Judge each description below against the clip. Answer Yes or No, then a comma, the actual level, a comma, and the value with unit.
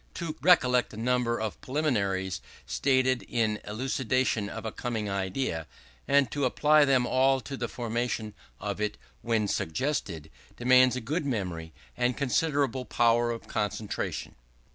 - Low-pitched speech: Yes, low, 120 Hz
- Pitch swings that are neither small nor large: Yes, average, 3.8 semitones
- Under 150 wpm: Yes, average, 140 wpm